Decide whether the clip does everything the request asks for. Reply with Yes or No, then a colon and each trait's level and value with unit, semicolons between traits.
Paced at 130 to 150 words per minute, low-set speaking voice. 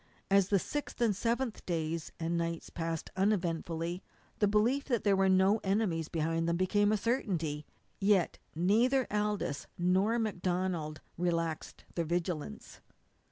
No: average, 140 wpm; medium, 185 Hz